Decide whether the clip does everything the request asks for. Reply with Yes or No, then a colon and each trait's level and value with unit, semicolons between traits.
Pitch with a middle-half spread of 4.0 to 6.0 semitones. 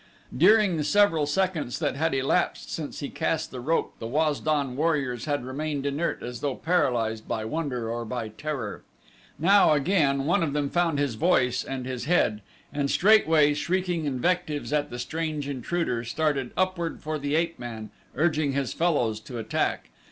Yes: average, 4.5 semitones